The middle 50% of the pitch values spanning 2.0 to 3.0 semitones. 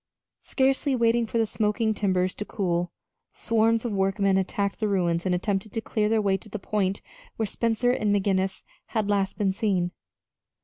Yes: narrow, 2.6 semitones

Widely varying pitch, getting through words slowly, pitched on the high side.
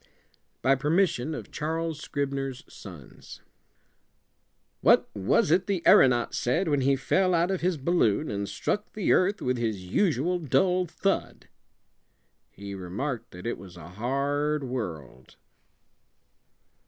No: wide, 7.5 semitones; slow, 130 wpm; medium, 140 Hz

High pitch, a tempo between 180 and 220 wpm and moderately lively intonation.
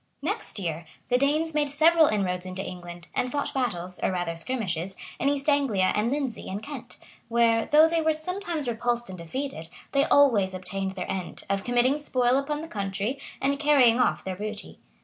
No: high, 240 Hz; average, 190 wpm; wide, 7.0 semitones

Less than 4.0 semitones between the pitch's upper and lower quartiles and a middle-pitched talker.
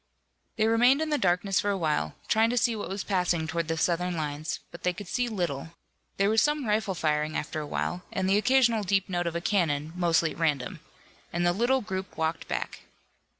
No: average, 4.9 semitones; medium, 180 Hz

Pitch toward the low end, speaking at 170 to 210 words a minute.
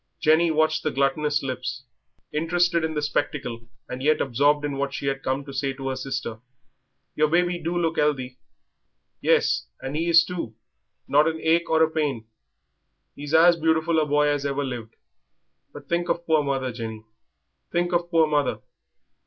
No: medium, 150 Hz; average, 175 wpm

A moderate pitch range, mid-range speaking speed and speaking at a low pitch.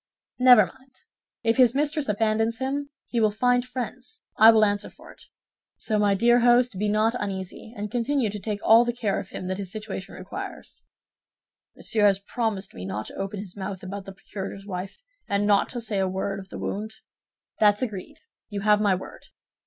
No: average, 3.3 semitones; average, 195 wpm; high, 210 Hz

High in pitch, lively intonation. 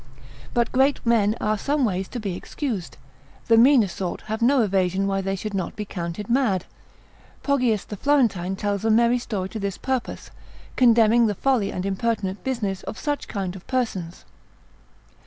No: high, 215 Hz; average, 3.9 semitones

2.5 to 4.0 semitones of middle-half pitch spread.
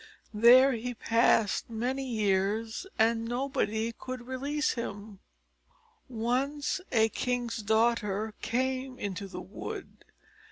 Yes: average, 2.8 semitones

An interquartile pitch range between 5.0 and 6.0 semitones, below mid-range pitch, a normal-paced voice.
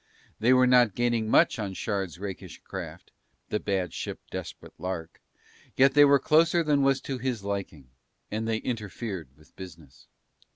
Yes: wide, 5.4 semitones; low, 110 Hz; average, 160 wpm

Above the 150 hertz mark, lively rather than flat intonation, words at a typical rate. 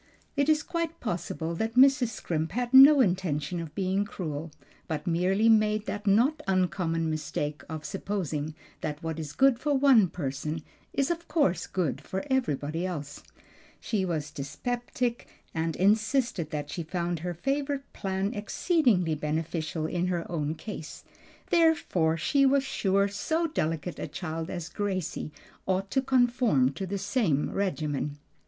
Yes: medium, 185 Hz; wide, 7.1 semitones; average, 145 wpm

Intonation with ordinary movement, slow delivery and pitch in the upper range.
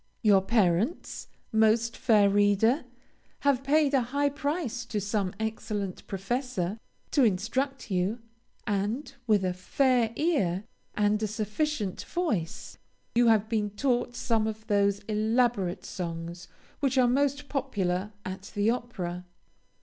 Yes: average, 4.3 semitones; slow, 125 wpm; high, 220 Hz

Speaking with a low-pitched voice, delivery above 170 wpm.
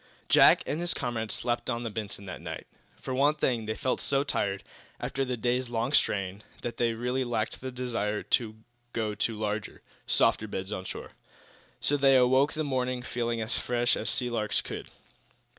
Yes: low, 120 Hz; average, 190 wpm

